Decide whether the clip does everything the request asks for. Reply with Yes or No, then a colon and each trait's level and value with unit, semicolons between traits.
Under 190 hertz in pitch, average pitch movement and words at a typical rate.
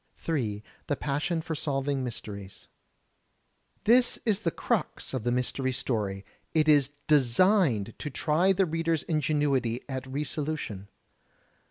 No: medium, 140 Hz; average, 4.6 semitones; slow, 130 wpm